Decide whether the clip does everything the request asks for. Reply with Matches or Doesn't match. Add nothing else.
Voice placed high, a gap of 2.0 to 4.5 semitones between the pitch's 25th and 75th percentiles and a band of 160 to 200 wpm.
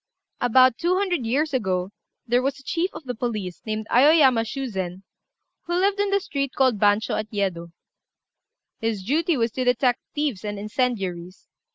Doesn't match